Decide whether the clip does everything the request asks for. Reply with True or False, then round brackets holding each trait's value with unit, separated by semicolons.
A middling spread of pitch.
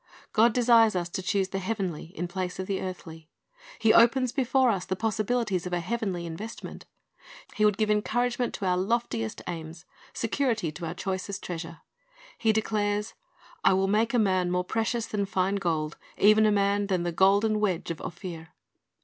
True (3.6 semitones)